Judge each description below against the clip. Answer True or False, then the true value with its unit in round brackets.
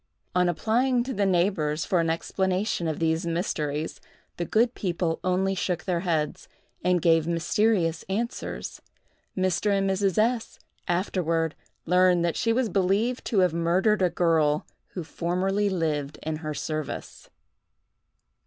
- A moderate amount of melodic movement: True (3.1 semitones)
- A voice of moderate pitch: True (180 Hz)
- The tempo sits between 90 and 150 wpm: True (140 wpm)